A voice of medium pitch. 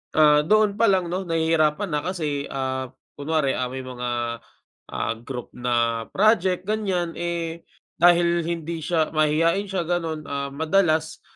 Yes: medium, 160 Hz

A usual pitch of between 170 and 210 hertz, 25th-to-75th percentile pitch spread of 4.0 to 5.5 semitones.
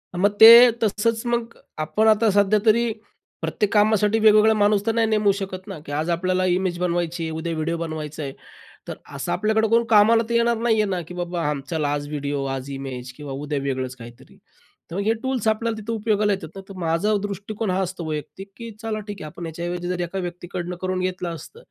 Yes: medium, 185 Hz; average, 4.7 semitones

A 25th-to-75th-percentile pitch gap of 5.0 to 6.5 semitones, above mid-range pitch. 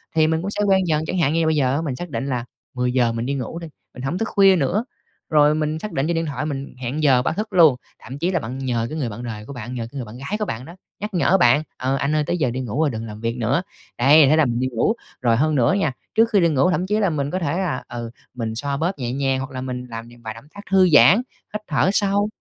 No: average, 5.3 semitones; medium, 140 Hz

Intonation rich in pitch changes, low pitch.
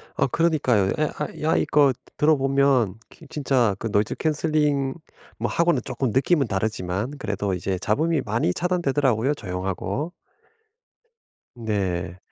Yes: wide, 6.4 semitones; low, 130 Hz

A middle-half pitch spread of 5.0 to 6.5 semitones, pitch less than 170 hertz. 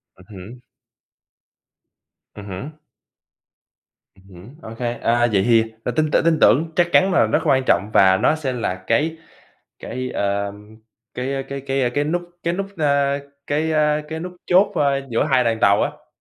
Yes: wide, 5.4 semitones; low, 135 Hz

